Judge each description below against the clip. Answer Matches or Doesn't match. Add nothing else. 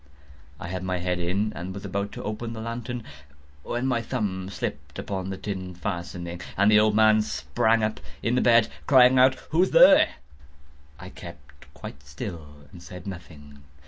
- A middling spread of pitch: Matches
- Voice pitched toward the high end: Doesn't match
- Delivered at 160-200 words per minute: Matches